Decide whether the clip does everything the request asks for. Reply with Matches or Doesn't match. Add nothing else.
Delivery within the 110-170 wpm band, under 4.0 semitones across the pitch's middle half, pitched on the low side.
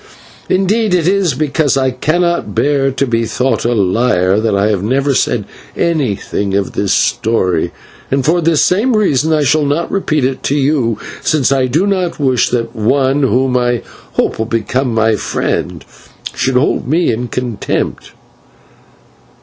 Doesn't match